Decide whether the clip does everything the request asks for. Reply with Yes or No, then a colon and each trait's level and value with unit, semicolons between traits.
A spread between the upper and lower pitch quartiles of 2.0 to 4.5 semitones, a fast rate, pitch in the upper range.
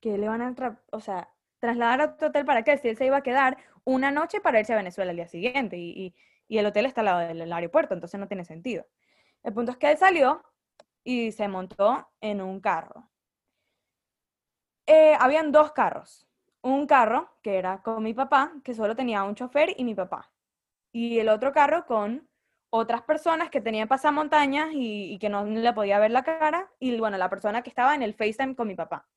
No: wide, 5.6 semitones; fast, 215 wpm; high, 240 Hz